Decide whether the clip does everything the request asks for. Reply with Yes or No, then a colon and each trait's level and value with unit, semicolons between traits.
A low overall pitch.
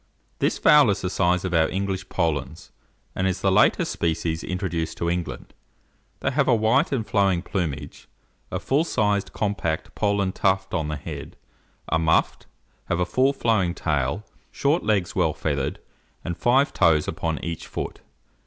Yes: very low, 95 Hz